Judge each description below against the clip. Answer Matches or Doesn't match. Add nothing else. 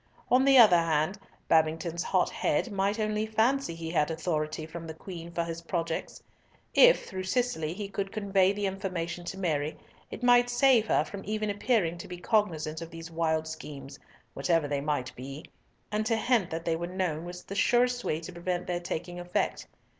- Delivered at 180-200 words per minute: Matches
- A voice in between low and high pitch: Matches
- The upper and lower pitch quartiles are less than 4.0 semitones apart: Doesn't match